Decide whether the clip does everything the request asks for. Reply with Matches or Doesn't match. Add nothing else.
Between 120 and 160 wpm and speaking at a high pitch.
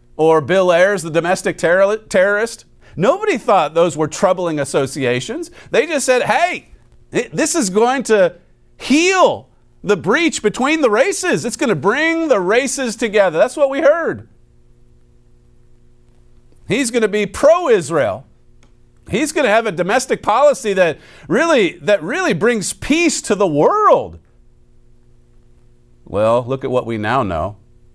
Matches